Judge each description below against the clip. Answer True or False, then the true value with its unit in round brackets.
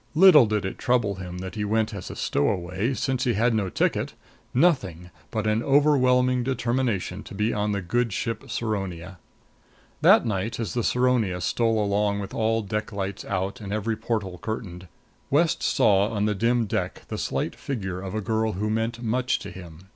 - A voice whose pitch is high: False (110 Hz)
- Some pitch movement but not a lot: True (3.7 semitones)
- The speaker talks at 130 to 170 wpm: False (185 wpm)